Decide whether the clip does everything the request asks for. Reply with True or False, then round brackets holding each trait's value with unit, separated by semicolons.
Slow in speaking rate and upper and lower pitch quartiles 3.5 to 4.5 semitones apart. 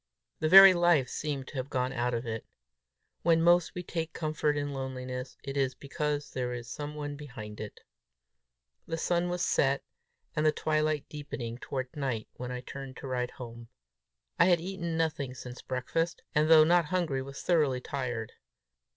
False (175 wpm; 4.1 semitones)